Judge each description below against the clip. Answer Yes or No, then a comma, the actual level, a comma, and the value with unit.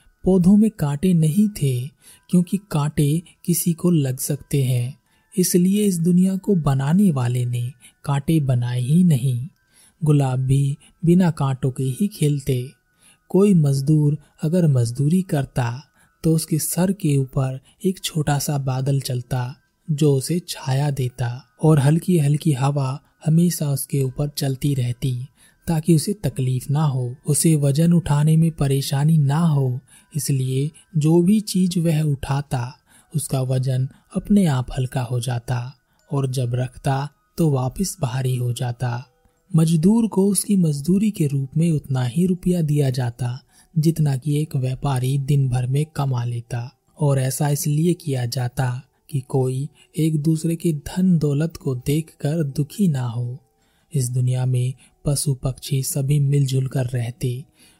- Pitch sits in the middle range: Yes, medium, 145 Hz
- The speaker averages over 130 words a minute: Yes, average, 145 wpm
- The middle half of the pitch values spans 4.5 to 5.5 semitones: No, average, 3.9 semitones